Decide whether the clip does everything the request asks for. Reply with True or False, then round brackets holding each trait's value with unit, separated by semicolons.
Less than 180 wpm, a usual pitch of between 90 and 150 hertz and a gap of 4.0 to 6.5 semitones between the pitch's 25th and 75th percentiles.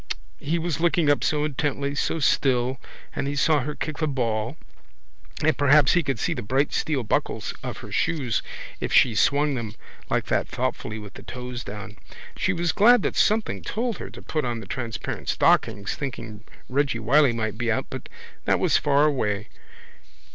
False (185 wpm; 135 Hz; 4.6 semitones)